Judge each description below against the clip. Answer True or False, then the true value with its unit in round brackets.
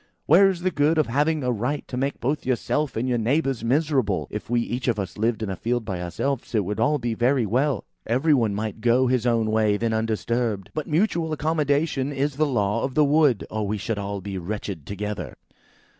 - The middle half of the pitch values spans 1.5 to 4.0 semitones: False (5.1 semitones)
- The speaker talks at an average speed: False (220 wpm)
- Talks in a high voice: False (120 Hz)